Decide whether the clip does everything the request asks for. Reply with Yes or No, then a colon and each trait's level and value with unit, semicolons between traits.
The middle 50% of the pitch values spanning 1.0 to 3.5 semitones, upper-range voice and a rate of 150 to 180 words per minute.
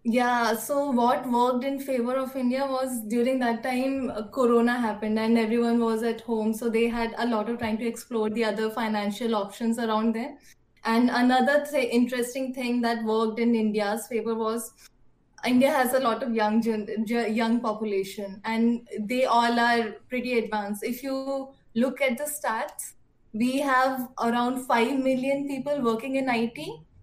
Yes: narrow, 2.4 semitones; high, 235 Hz; average, 165 wpm